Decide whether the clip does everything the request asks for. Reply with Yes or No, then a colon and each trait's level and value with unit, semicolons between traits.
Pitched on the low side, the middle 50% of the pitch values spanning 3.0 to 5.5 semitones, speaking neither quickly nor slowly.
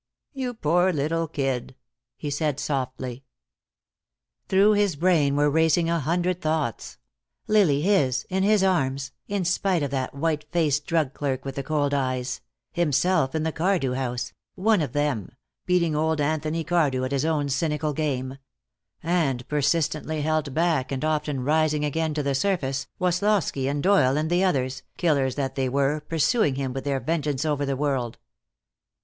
No: medium, 150 Hz; average, 3.6 semitones; average, 160 wpm